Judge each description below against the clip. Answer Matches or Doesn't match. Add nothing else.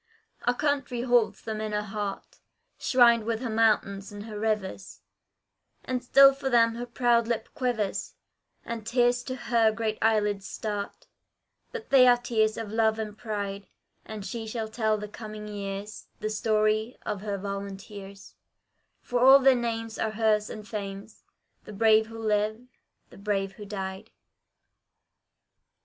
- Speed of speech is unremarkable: Matches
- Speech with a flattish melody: Matches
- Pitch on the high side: Matches